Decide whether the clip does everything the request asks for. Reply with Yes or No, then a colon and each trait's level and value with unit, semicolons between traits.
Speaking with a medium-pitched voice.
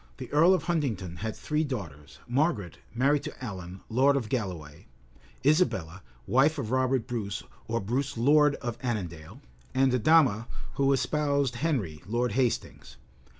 No: low, 125 Hz